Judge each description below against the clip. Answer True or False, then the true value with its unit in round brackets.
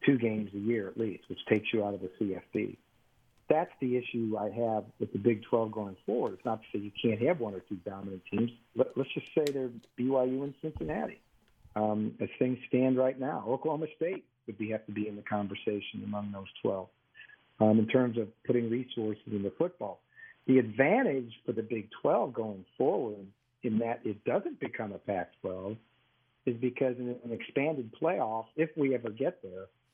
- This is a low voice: True (115 Hz)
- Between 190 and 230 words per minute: True (200 wpm)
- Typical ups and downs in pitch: True (3.3 semitones)